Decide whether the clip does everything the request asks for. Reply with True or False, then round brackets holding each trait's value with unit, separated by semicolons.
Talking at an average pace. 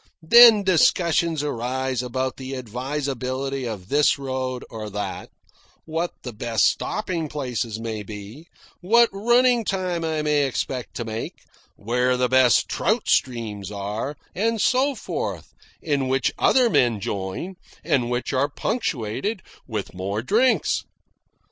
False (130 wpm)